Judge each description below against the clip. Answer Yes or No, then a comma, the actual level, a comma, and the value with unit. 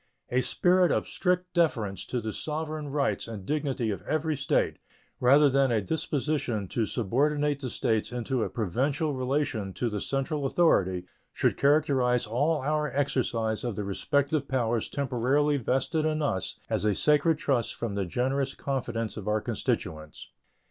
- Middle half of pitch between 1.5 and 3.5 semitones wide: No, average, 4.7 semitones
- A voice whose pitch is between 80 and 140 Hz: Yes, low, 135 Hz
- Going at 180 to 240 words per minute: No, average, 155 wpm